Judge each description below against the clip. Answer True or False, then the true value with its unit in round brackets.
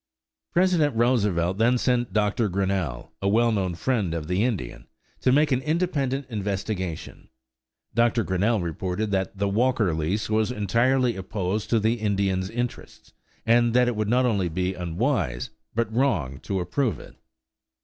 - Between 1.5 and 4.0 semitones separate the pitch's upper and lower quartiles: False (4.6 semitones)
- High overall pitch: False (105 Hz)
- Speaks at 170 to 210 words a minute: False (150 wpm)